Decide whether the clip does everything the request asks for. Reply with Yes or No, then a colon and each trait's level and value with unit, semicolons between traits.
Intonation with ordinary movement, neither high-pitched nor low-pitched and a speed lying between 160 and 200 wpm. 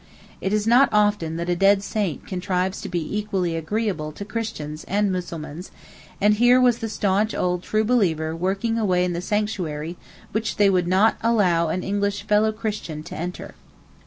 No: average, 3.5 semitones; high, 195 Hz; average, 175 wpm